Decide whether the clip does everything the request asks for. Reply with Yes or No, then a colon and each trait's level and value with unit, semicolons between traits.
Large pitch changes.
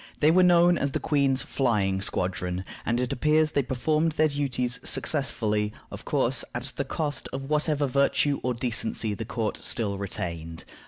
Yes: wide, 5.7 semitones